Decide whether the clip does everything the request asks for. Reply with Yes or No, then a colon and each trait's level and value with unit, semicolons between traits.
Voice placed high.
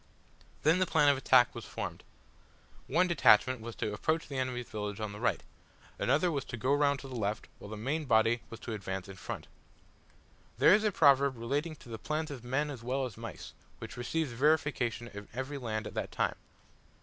No: low, 130 Hz